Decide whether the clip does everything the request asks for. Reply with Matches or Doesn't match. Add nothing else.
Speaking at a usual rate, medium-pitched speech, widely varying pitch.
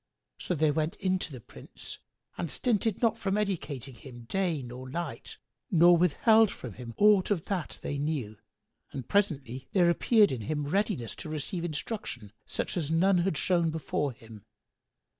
Matches